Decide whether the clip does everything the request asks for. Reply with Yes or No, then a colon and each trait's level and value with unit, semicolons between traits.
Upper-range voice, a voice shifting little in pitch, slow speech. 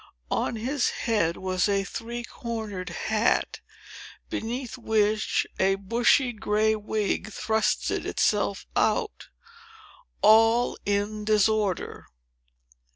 Yes: high, 215 Hz; narrow, 2.2 semitones; slow, 95 wpm